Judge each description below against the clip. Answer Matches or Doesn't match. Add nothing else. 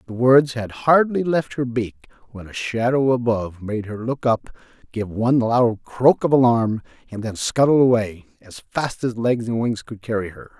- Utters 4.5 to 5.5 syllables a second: Matches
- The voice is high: Doesn't match